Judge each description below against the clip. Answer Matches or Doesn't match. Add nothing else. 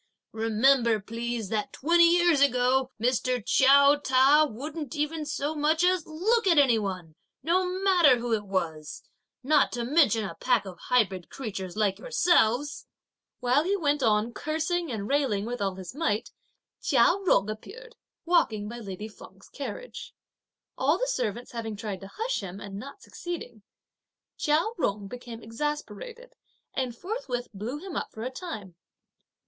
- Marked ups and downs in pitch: Matches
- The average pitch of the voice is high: Matches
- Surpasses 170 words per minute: Doesn't match